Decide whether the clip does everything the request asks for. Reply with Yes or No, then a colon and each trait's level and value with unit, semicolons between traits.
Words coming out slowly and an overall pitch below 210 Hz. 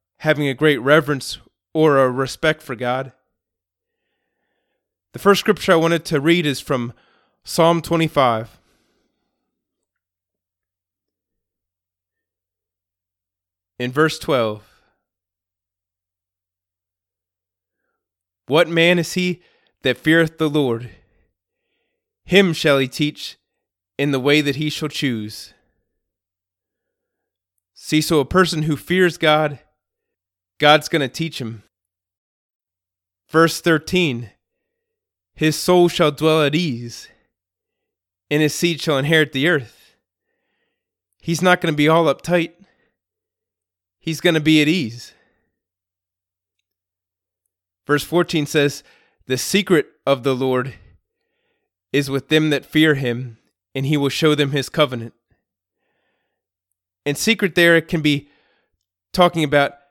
Yes: slow, 110 wpm; low, 135 Hz